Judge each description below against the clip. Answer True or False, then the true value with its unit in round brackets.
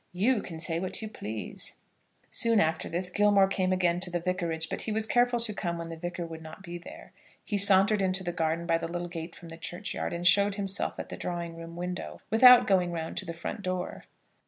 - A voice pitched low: False (180 Hz)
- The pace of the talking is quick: True (230 wpm)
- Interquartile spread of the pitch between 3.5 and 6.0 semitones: False (3.0 semitones)